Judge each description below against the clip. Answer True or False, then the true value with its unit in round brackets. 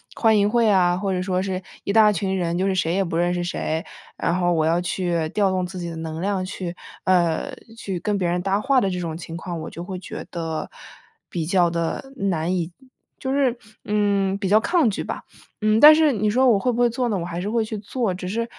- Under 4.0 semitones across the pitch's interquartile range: True (3.4 semitones)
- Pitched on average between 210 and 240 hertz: False (190 Hz)